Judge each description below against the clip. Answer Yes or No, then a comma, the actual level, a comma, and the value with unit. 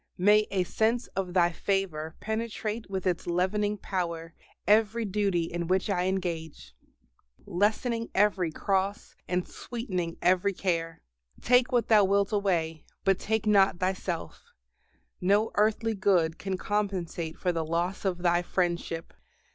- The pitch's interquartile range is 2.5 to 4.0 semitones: Yes, average, 3.2 semitones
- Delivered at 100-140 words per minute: Yes, slow, 135 wpm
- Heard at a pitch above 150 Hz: Yes, high, 190 Hz